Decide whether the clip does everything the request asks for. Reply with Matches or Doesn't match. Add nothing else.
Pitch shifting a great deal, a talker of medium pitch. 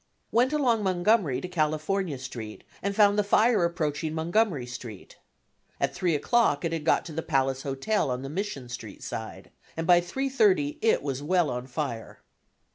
Matches